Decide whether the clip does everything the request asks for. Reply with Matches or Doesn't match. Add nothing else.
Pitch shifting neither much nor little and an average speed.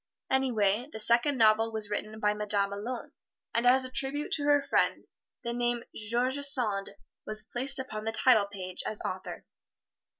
Matches